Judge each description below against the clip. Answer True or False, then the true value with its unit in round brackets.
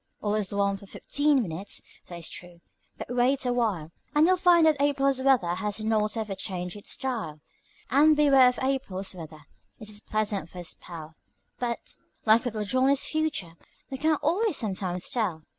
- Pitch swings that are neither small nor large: False (6.5 semitones)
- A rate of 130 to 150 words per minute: False (175 wpm)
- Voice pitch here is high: True (220 Hz)